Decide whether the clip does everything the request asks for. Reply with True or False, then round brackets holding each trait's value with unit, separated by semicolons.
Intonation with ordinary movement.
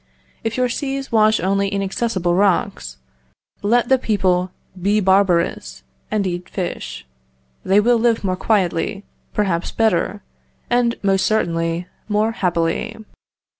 True (3.7 semitones)